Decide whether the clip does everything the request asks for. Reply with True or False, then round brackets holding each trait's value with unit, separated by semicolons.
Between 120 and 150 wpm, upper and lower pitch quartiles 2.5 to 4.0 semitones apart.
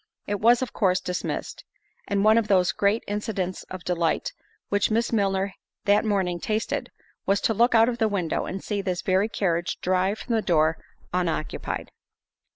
False (165 wpm; 3.0 semitones)